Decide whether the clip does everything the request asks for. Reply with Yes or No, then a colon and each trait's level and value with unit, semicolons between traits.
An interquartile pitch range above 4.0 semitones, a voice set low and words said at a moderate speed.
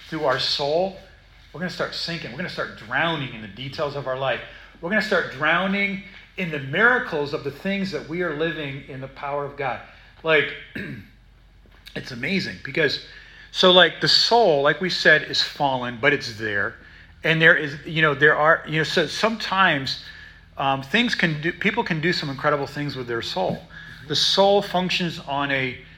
No: average, 4.9 semitones; medium, 155 Hz; average, 195 wpm